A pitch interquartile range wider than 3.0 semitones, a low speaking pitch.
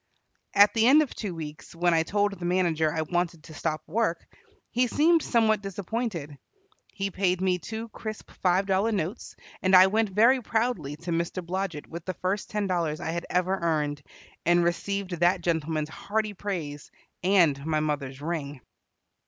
No: average, 4.0 semitones; medium, 180 Hz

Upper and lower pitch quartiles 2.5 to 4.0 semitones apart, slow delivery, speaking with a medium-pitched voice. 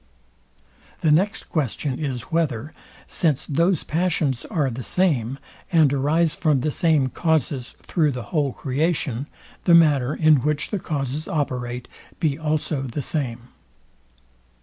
Yes: average, 3.5 semitones; slow, 130 wpm; medium, 150 Hz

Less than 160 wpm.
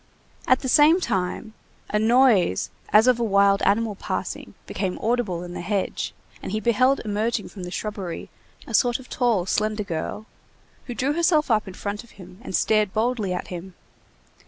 No: average, 180 wpm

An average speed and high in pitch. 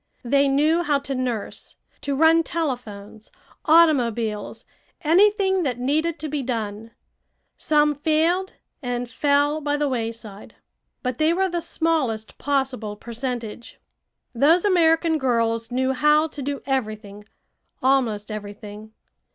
No: slow, 120 wpm; very high, 270 Hz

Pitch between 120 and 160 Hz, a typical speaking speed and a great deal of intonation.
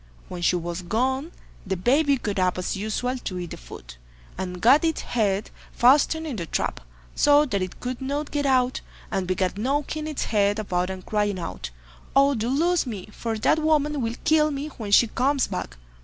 No: high, 235 Hz; average, 195 wpm; wide, 7.2 semitones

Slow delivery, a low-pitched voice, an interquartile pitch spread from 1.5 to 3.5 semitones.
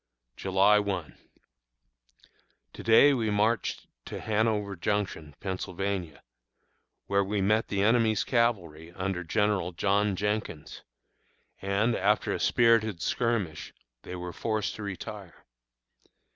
Yes: slow, 110 wpm; low, 100 Hz; average, 2.9 semitones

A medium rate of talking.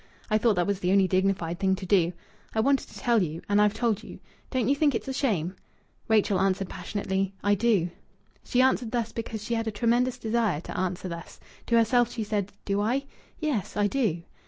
No: fast, 210 wpm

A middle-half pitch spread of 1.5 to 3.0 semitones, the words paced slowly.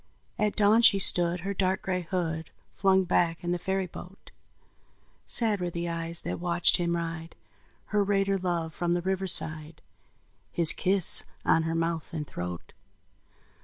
No: narrow, 2.5 semitones; average, 155 wpm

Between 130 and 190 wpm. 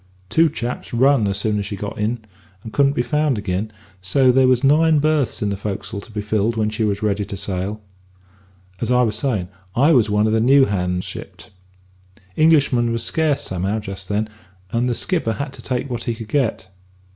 No: fast, 205 wpm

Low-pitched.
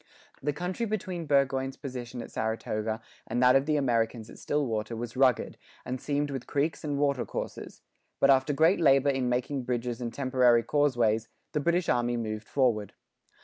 Yes: low, 130 Hz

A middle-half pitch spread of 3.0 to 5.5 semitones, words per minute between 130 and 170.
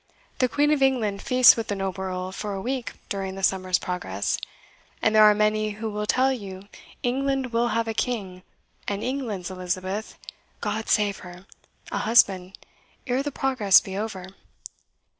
Yes: average, 4.4 semitones; average, 165 wpm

